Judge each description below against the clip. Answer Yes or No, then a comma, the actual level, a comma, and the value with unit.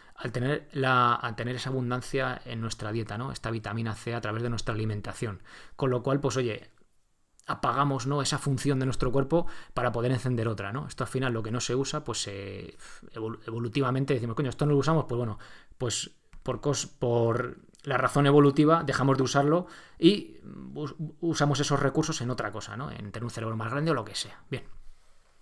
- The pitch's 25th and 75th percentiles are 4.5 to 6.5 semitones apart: No, average, 3.5 semitones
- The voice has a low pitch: Yes, low, 125 Hz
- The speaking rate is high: Yes, fast, 200 wpm